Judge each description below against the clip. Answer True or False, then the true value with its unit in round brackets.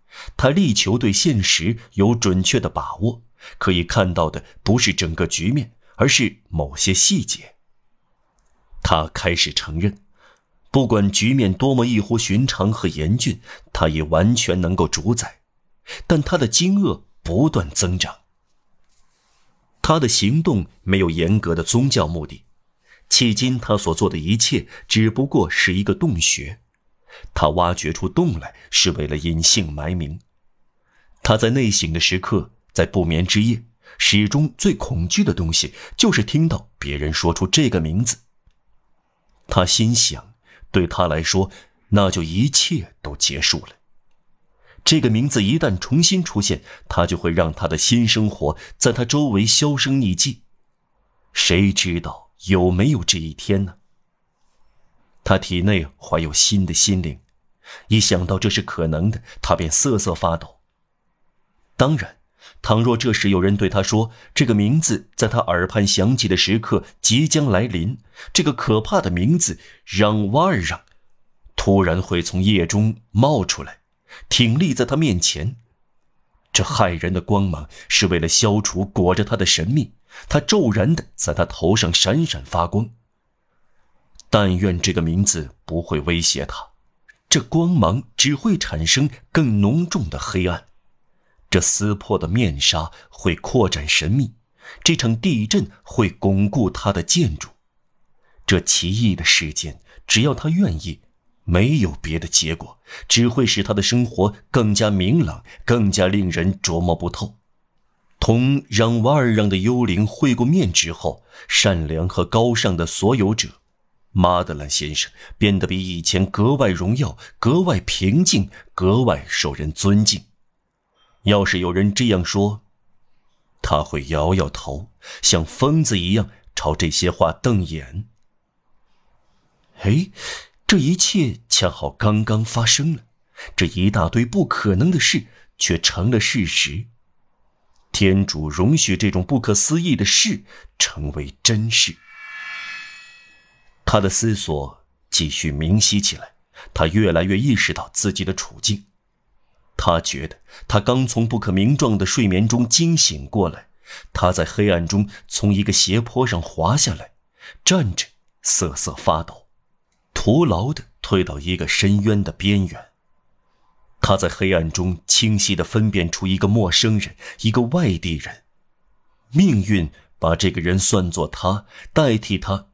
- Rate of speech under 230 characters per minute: True (205 characters per minute)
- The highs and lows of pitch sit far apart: False (4.7 semitones)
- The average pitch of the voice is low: True (100 Hz)